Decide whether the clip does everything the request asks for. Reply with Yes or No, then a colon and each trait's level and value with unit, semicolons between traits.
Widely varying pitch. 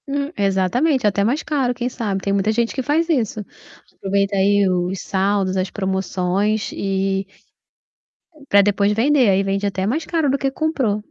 No: average, 4.8 semitones